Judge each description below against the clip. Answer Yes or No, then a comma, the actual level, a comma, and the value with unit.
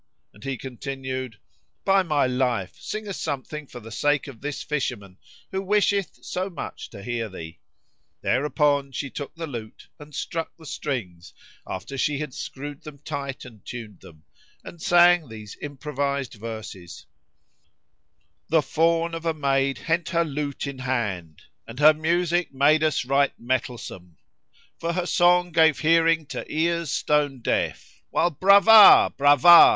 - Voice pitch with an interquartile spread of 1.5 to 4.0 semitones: No, average, 4.9 semitones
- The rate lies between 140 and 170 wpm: Yes, average, 155 wpm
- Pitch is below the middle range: No, medium, 145 Hz